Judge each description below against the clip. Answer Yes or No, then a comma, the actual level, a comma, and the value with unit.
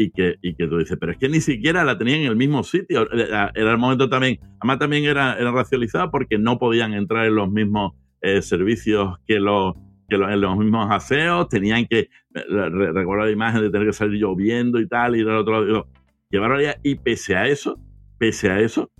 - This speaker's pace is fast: Yes, fast, 215 wpm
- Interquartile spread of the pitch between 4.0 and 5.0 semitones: No, average, 3.4 semitones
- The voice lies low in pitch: Yes, low, 110 Hz